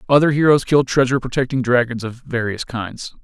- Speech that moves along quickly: No, average, 165 wpm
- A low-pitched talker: Yes, low, 125 Hz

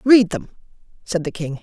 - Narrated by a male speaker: Yes, male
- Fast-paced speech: No, average, 185 wpm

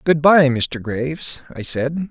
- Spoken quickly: No, average, 170 wpm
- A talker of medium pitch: Yes, medium, 145 Hz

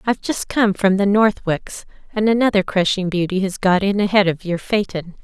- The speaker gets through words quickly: No, average, 195 wpm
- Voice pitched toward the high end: Yes, high, 195 Hz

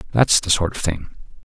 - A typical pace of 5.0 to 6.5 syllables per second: Yes, 5.5 syllables/s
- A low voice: Yes, very low, 80 Hz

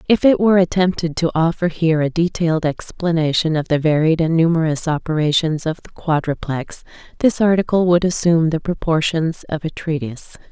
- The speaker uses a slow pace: No, average, 160 wpm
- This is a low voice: No, medium, 165 Hz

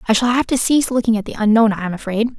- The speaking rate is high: Yes, fast, 300 wpm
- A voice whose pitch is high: Yes, high, 225 Hz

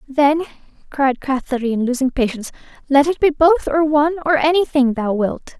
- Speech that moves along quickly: No, average, 160 wpm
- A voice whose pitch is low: No, very high, 280 Hz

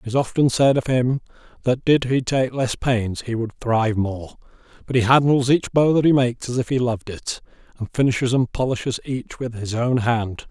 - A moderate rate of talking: No, fast, 215 wpm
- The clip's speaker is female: No, male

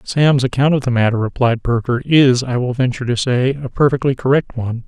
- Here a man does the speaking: Yes, male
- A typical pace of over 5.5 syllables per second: Yes, 5.7 syllables/s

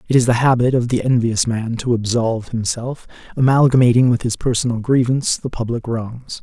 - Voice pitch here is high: No, low, 120 Hz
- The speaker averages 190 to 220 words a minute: No, average, 175 wpm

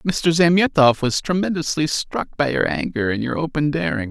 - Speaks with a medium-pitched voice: Yes, medium, 145 Hz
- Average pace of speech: Yes, average, 175 wpm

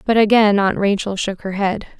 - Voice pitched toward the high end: Yes, high, 200 Hz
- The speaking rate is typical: No, fast, 210 wpm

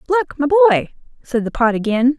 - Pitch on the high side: Yes, very high, 260 Hz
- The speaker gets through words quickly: No, average, 190 wpm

